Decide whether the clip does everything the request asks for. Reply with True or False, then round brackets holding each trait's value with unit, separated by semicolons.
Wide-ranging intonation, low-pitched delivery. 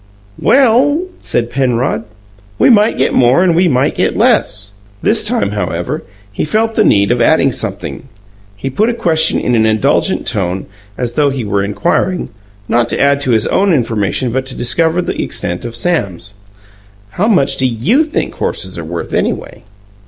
True (8.0 semitones; 130 Hz)